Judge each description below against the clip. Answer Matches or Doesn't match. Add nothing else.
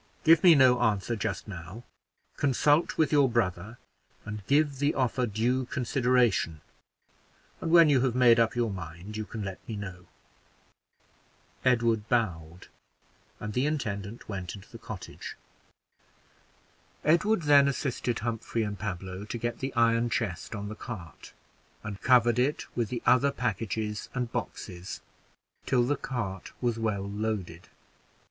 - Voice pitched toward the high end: Doesn't match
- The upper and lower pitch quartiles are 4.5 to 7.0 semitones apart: Doesn't match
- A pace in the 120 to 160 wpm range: Matches